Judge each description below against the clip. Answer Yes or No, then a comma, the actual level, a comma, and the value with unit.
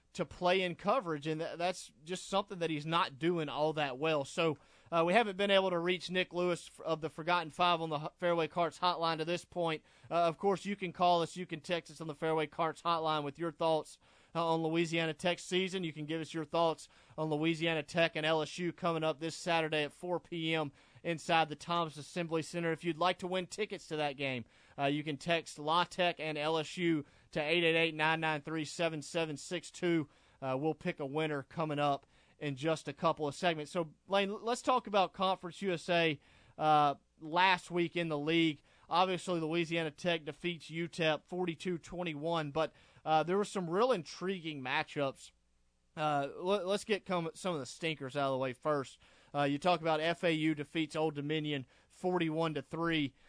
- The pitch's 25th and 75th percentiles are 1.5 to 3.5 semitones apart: Yes, narrow, 2.4 semitones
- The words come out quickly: No, average, 190 wpm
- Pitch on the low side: No, medium, 165 Hz